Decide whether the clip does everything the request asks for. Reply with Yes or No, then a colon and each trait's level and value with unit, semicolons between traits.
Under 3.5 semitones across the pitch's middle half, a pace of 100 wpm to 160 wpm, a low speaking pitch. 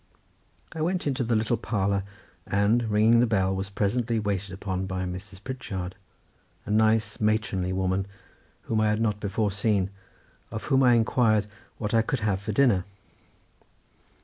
Yes: average, 2.8 semitones; average, 155 wpm; low, 105 Hz